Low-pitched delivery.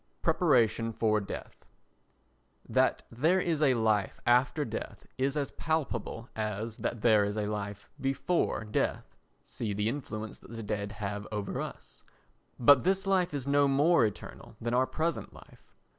Yes: low, 115 Hz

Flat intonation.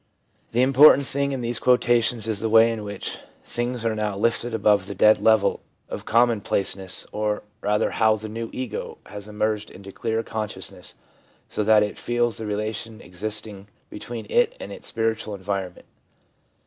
Yes: narrow, 1.9 semitones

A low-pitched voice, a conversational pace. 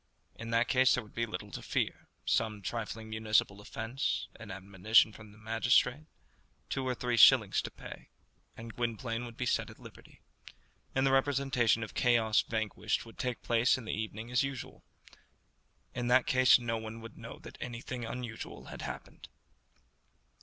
Yes: low, 115 Hz; average, 165 wpm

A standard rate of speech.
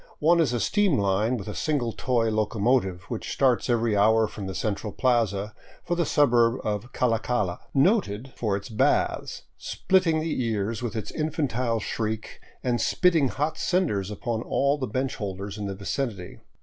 Yes: average, 170 wpm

